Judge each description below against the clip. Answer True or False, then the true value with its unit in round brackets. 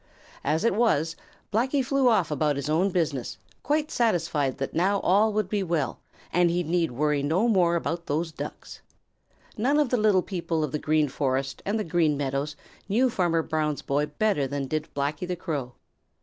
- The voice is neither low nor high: True (165 Hz)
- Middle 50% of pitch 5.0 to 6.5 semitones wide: True (5.5 semitones)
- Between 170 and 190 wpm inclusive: True (185 wpm)